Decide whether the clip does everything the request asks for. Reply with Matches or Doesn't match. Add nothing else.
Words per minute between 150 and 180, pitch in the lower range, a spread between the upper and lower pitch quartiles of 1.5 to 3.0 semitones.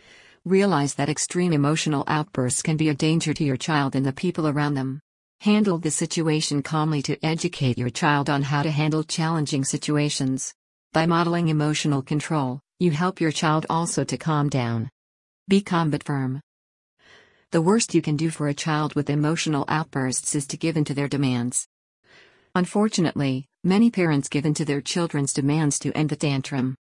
Doesn't match